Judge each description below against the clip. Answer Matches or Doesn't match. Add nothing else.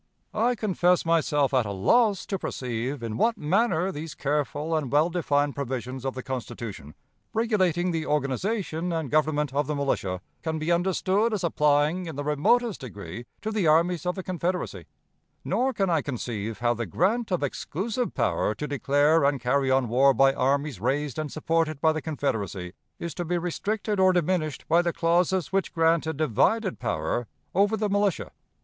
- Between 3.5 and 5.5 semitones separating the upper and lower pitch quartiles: Matches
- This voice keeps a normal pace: Matches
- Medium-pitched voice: Matches